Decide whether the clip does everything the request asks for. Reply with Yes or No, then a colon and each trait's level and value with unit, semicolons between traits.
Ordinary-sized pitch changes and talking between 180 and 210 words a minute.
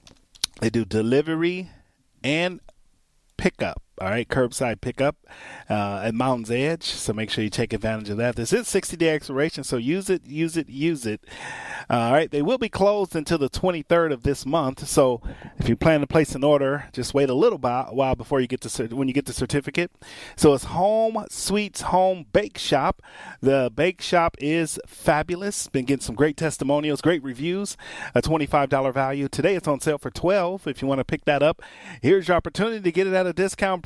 Yes: average, 4.6 semitones; average, 200 wpm